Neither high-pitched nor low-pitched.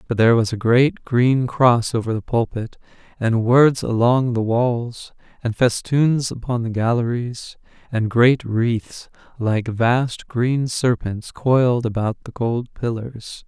No: low, 120 Hz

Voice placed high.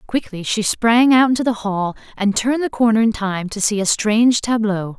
Yes: high, 220 Hz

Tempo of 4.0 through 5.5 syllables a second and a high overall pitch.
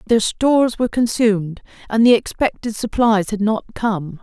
Yes: 4.9 syllables/s; high, 220 Hz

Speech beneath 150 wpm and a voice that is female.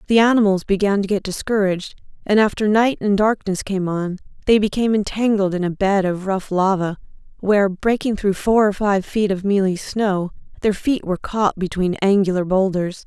No: average, 180 wpm; female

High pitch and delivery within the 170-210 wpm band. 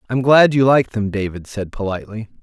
No: low, 115 Hz; average, 200 wpm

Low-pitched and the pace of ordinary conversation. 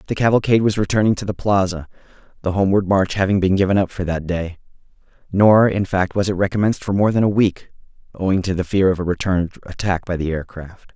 No: very low, 95 Hz; fast, 220 wpm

